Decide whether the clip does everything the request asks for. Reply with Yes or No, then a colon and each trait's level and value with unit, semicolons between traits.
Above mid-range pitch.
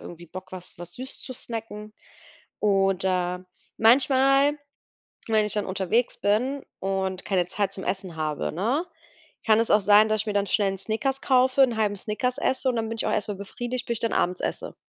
Yes: high, 210 Hz